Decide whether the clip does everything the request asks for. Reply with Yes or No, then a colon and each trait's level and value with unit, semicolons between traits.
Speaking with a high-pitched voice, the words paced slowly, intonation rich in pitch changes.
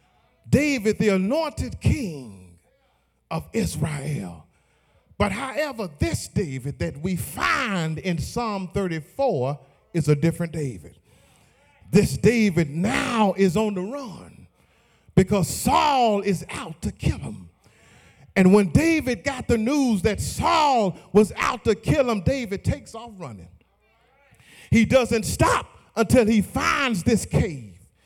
Yes: high, 195 Hz; slow, 125 wpm; wide, 7.4 semitones